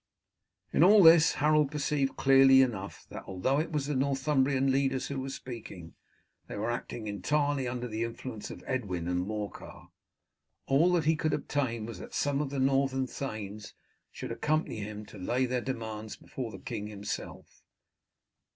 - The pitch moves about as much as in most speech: Yes, average, 4.6 semitones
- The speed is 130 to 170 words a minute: Yes, average, 165 wpm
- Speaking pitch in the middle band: No, low, 130 Hz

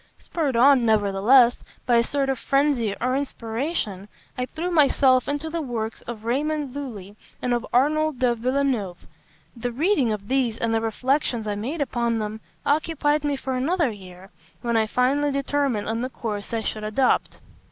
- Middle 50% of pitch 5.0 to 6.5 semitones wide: No, average, 4.2 semitones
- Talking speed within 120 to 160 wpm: No, average, 170 wpm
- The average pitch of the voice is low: No, very high, 250 Hz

